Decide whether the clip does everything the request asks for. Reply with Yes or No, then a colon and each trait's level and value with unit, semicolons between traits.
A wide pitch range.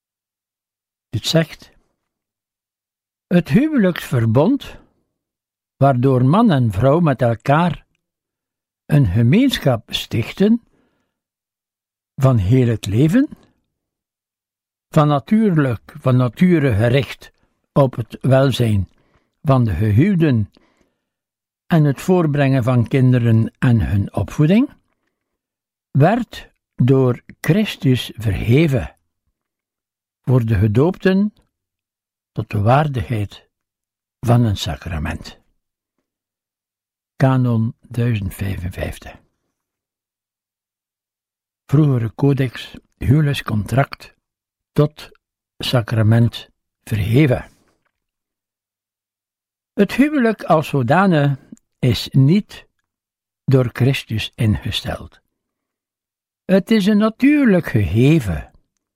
Yes: wide, 5.9 semitones